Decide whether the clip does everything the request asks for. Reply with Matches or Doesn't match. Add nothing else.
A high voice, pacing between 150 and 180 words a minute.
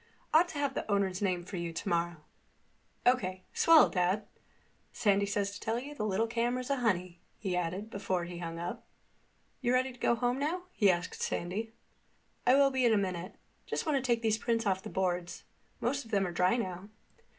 Doesn't match